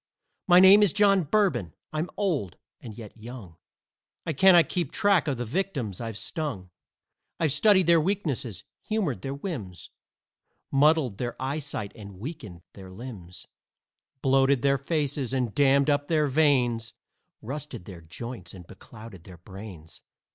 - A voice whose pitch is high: No, low, 135 Hz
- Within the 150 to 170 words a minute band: No, average, 140 wpm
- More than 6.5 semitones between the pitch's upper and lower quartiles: Yes, wide, 7.0 semitones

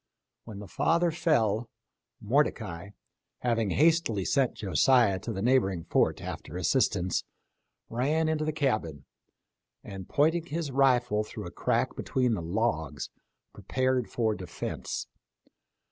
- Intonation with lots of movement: Yes, wide, 6.2 semitones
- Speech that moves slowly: Yes, slow, 120 wpm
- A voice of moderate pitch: No, low, 120 Hz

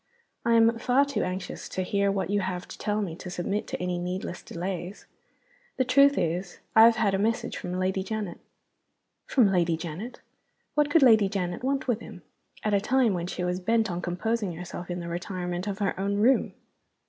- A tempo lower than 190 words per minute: No, average, 200 wpm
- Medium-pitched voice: No, high, 195 Hz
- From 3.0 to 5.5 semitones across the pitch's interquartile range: Yes, average, 4.0 semitones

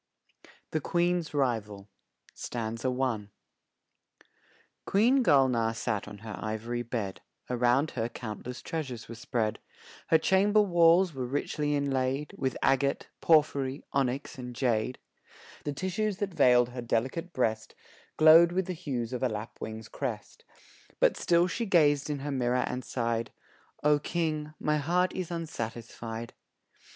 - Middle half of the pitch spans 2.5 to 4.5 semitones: No, wide, 5.6 semitones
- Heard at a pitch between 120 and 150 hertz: Yes, low, 135 Hz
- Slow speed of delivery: Yes, slow, 130 wpm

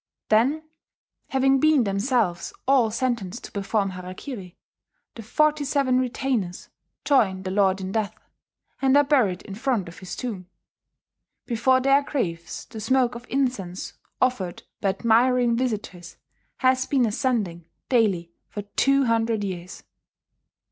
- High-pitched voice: Yes, high, 230 Hz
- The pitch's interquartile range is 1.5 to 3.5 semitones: No, average, 5.2 semitones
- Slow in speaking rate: Yes, slow, 130 wpm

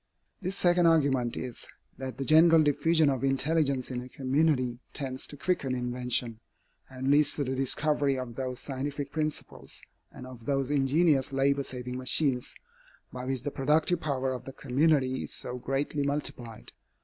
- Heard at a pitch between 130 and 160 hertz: Yes, low, 135 Hz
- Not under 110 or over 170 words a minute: Yes, average, 160 wpm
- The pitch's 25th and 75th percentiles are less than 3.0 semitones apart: Yes, narrow, 2.5 semitones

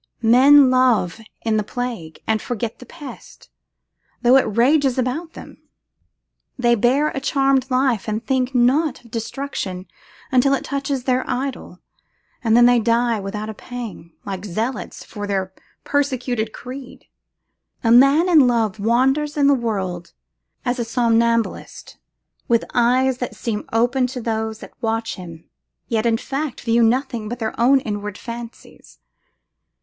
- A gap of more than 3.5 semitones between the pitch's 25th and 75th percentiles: No, average, 3.0 semitones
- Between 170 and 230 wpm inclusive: No, average, 145 wpm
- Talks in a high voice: Yes, high, 240 Hz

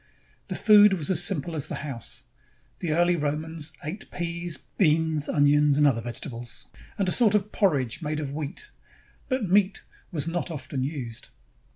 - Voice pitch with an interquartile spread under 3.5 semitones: No, average, 3.8 semitones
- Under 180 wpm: Yes, average, 165 wpm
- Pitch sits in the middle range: Yes, medium, 155 Hz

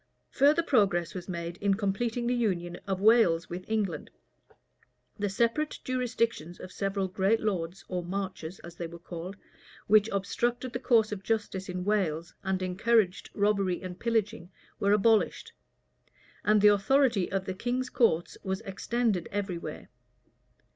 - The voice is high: Yes, high, 200 Hz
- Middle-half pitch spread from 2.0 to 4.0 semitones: Yes, average, 3.7 semitones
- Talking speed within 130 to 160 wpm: Yes, average, 145 wpm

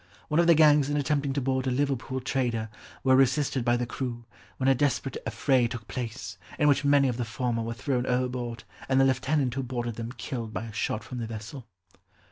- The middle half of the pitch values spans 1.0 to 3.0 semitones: Yes, narrow, 2.5 semitones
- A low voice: Yes, low, 130 Hz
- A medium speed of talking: No, fast, 215 wpm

